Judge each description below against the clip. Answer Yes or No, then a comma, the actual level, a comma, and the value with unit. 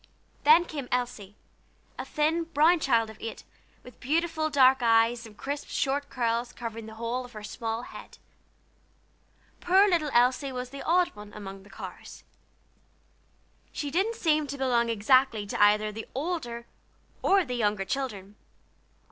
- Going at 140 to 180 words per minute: Yes, average, 150 wpm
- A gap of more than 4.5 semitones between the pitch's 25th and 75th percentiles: Yes, average, 4.9 semitones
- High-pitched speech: Yes, very high, 250 Hz